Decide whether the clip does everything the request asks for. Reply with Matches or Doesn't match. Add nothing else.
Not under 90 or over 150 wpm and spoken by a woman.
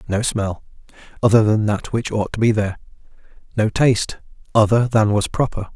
Doesn't match